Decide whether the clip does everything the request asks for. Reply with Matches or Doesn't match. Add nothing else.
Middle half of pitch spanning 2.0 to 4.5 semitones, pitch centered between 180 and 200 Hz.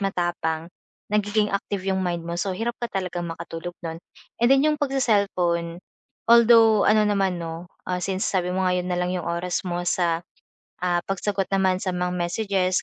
Matches